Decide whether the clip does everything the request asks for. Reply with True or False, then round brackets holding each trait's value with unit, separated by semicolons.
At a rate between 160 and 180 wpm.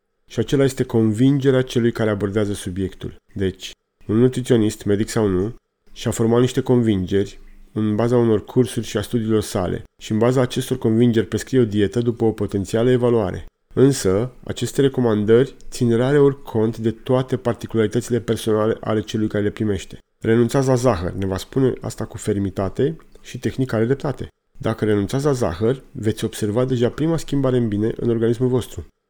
True (165 wpm)